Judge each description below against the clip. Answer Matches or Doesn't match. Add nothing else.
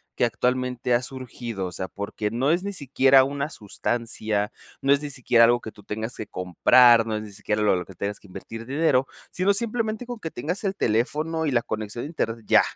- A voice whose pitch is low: Matches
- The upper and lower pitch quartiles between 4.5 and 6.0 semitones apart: Matches